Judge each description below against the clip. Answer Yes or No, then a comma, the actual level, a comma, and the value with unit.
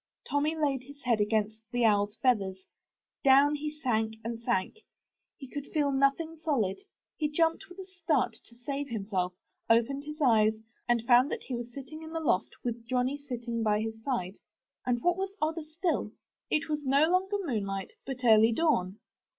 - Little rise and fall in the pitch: No, average, 5.3 semitones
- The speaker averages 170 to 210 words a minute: Yes, average, 180 wpm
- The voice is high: Yes, very high, 255 Hz